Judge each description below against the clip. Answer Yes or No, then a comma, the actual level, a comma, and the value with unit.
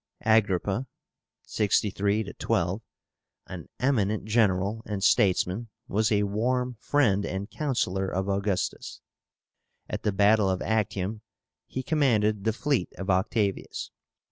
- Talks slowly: Yes, slow, 115 wpm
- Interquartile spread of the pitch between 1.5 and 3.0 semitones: Yes, narrow, 2.5 semitones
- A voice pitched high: No, low, 105 Hz